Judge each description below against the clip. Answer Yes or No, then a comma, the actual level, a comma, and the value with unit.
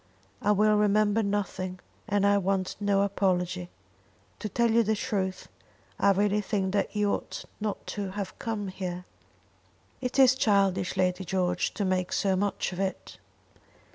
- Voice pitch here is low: No, high, 200 Hz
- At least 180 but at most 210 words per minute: No, average, 155 wpm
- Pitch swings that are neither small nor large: No, narrow, 1.8 semitones